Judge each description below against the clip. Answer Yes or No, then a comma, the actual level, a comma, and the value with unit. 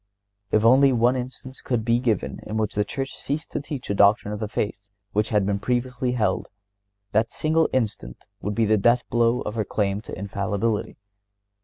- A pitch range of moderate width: Yes, average, 3.3 semitones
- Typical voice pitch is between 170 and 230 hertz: No, low, 115 Hz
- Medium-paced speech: Yes, average, 185 wpm